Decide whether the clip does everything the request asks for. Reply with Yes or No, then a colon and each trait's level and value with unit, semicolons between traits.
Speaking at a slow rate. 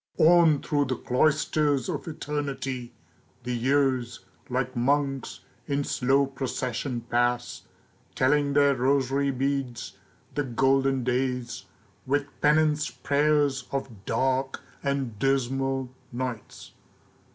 Yes: slow, 100 wpm